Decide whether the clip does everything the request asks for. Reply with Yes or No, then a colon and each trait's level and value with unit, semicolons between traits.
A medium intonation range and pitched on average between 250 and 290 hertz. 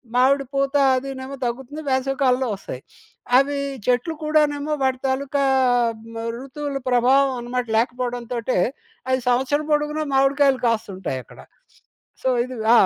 No: narrow, 2.1 semitones; very high, 265 Hz